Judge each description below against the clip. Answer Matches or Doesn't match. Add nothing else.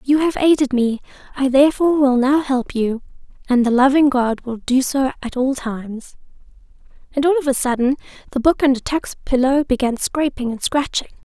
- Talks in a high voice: Matches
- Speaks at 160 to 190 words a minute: Matches